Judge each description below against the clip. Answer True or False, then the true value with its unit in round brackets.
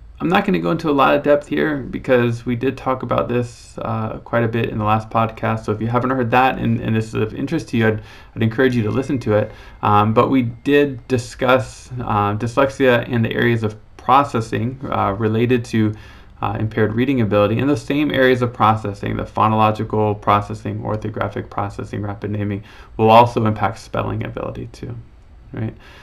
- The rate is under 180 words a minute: False (200 wpm)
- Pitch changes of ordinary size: True (3.0 semitones)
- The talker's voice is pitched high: False (115 Hz)